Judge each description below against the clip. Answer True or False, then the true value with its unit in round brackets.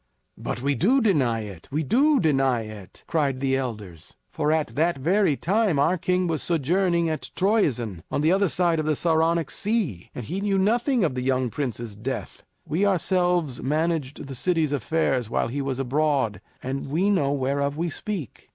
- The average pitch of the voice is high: False (150 Hz)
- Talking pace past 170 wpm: True (180 wpm)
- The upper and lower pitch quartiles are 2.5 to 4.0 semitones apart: False (5.4 semitones)